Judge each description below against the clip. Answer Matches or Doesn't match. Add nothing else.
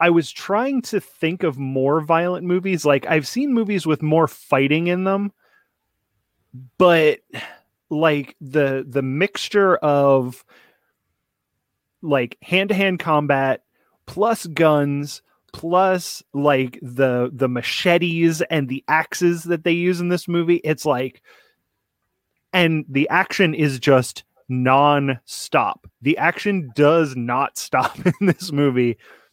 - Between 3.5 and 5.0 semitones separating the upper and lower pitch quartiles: Matches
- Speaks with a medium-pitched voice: Matches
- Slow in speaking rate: Matches